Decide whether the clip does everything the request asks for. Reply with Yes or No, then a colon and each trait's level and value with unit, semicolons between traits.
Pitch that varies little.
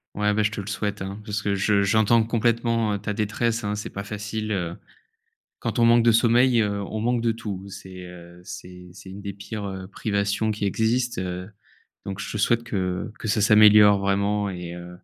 Yes: narrow, 2.2 semitones